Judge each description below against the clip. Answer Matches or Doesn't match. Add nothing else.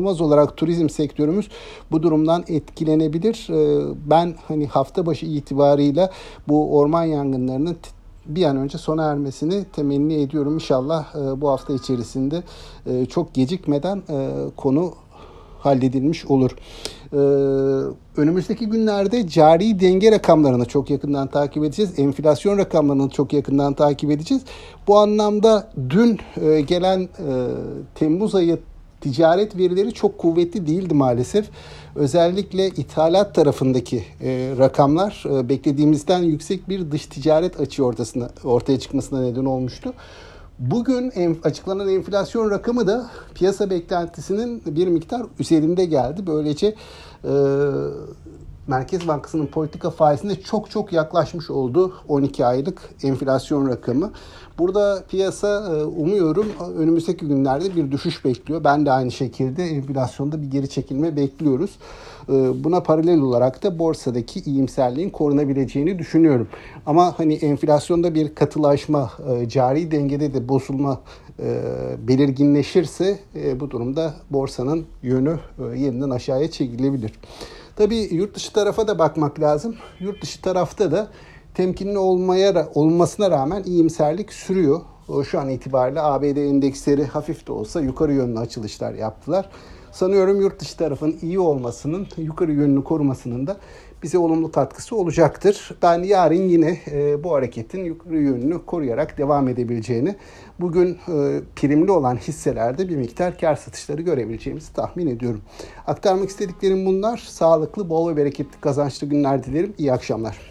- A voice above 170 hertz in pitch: Doesn't match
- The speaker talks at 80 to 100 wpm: Doesn't match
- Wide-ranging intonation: Doesn't match